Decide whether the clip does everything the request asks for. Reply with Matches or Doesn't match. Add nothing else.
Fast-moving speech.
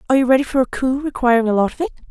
Matches